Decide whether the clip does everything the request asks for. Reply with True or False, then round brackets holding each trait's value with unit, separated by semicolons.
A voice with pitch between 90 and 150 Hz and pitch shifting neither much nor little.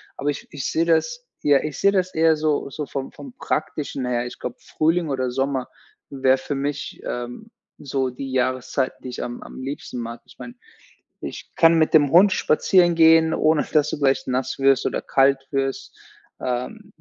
True (140 Hz; 3.7 semitones)